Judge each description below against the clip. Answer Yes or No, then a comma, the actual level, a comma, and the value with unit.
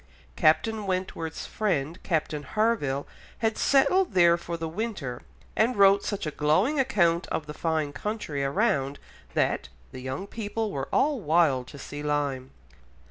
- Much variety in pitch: Yes, wide, 6.5 semitones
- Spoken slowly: No, average, 145 wpm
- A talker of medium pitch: Yes, medium, 170 Hz